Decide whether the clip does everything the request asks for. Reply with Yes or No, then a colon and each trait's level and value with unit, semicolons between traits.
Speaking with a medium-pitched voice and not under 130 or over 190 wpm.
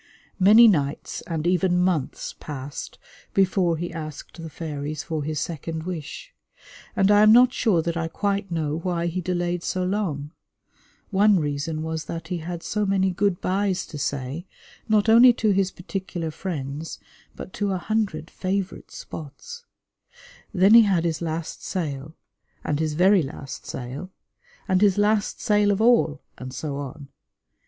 Yes: medium, 175 Hz; average, 160 wpm